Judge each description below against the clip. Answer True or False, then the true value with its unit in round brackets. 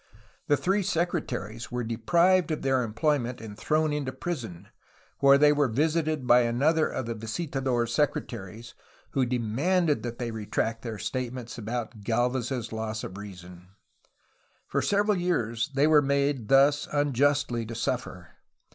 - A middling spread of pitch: True (4.5 semitones)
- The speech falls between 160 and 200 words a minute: False (145 wpm)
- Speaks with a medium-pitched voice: False (130 Hz)